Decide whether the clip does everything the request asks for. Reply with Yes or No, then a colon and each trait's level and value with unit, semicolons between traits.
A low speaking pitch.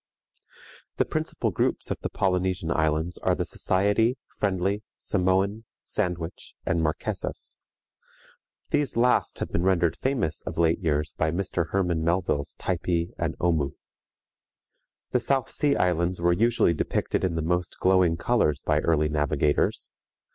Yes: very low, 85 Hz